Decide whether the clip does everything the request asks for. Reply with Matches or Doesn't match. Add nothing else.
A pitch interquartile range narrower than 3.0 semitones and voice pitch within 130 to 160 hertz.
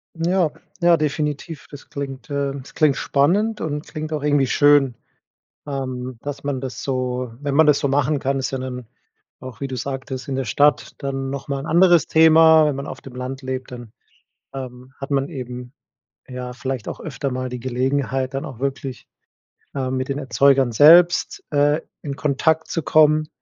Matches